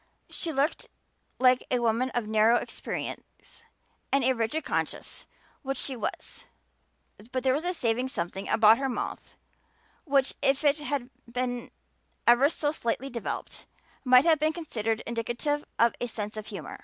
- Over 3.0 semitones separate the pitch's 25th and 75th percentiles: Yes, average, 3.5 semitones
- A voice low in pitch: No, very high, 250 Hz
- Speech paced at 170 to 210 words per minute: No, average, 150 wpm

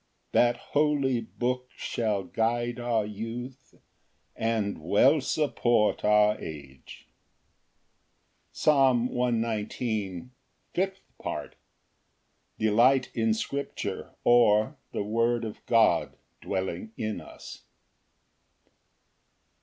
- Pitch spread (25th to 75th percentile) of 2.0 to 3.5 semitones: Yes, average, 2.9 semitones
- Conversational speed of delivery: No, slow, 85 wpm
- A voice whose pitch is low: Yes, low, 115 Hz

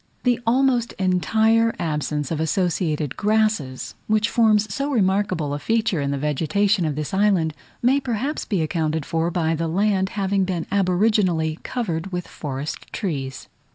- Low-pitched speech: No, medium, 185 Hz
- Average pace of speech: Yes, average, 150 wpm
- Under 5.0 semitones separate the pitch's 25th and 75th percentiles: No, average, 5.3 semitones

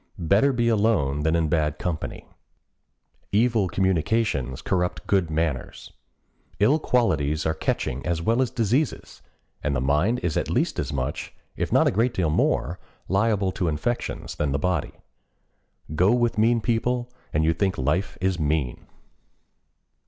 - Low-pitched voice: Yes, very low, 90 Hz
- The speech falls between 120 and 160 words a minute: Yes, average, 150 wpm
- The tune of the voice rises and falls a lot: Yes, wide, 6.8 semitones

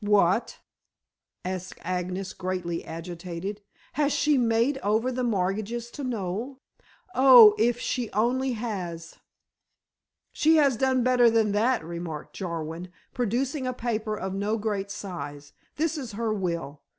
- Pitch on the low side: No, high, 215 Hz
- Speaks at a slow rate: Yes, slow, 130 wpm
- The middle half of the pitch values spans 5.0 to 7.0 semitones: Yes, average, 5.3 semitones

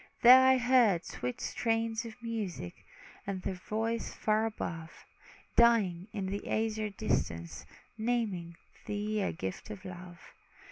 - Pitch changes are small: No, average, 4.1 semitones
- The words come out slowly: Yes, slow, 130 wpm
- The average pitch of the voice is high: Yes, high, 215 Hz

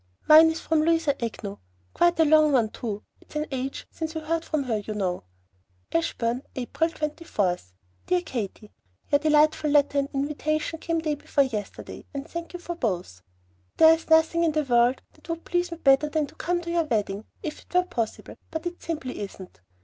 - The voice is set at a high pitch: Yes, very high, 300 Hz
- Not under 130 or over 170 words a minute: No, average, 195 wpm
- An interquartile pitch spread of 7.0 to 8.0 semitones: No, wide, 5.4 semitones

